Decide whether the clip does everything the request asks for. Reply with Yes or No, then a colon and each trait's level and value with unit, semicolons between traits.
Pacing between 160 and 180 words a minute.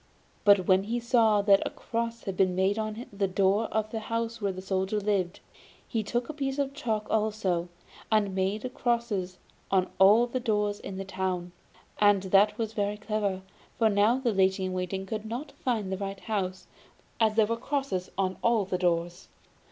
No: average, 190 wpm